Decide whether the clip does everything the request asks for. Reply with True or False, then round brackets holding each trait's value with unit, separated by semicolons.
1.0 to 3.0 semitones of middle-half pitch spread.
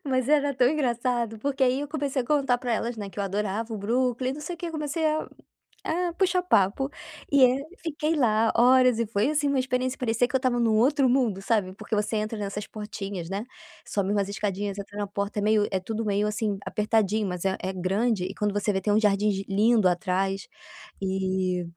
False (4.3 semitones)